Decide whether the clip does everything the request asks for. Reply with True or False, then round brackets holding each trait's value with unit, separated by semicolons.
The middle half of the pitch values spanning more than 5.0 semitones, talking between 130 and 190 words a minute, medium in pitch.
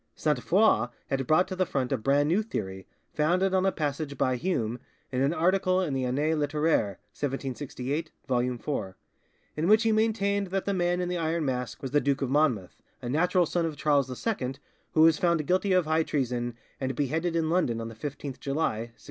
False (5.4 semitones; 205 wpm; 150 Hz)